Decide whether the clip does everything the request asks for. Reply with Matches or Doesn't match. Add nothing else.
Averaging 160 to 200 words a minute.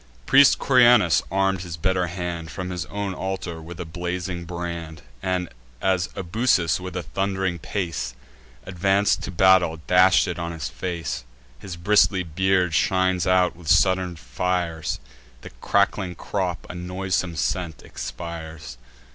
Doesn't match